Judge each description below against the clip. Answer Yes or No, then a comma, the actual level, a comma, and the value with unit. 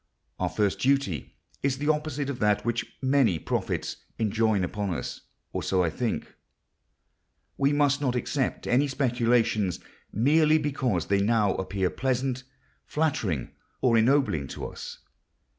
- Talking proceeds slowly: Yes, slow, 130 wpm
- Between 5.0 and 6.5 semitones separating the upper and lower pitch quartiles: Yes, wide, 5.5 semitones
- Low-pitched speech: Yes, low, 120 Hz